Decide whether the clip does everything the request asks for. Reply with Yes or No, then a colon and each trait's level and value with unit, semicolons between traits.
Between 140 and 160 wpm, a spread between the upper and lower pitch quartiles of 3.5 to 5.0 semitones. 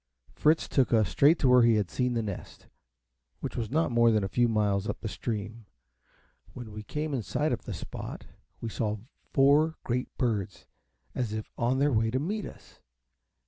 No: average, 190 wpm; average, 3.8 semitones